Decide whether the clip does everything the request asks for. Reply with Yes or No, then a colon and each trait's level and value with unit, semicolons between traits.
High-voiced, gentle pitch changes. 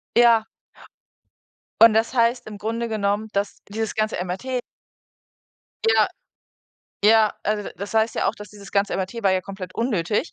Yes: high, 215 Hz; narrow, 2.3 semitones